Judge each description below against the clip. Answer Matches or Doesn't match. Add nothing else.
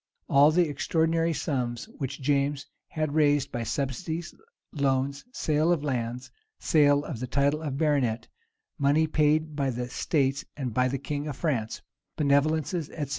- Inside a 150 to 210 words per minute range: Matches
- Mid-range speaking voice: Matches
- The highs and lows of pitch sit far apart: Doesn't match